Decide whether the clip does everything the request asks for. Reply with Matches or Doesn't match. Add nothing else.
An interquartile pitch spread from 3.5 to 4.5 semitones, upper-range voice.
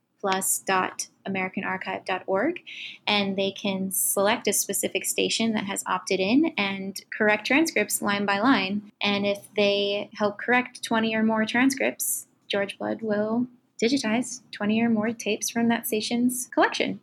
Doesn't match